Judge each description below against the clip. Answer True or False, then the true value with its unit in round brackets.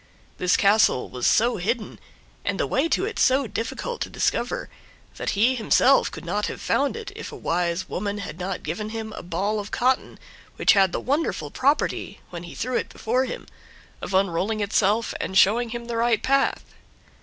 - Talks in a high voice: True (220 Hz)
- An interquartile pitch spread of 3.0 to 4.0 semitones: False (4.7 semitones)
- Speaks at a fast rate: False (190 wpm)